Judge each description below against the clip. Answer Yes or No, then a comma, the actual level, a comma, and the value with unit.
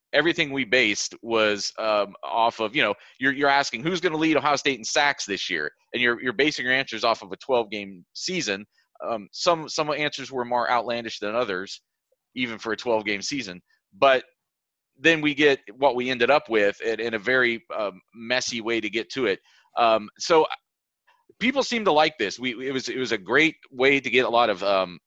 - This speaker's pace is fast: Yes, fast, 215 wpm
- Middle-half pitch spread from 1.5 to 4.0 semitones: No, average, 4.5 semitones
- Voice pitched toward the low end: Yes, low, 125 Hz